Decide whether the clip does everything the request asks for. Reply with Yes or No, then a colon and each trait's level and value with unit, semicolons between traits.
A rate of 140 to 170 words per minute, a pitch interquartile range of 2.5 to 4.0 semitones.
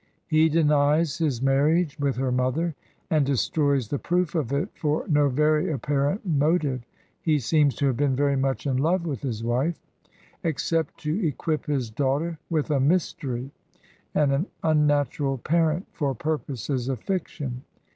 Yes: average, 160 wpm; average, 2.8 semitones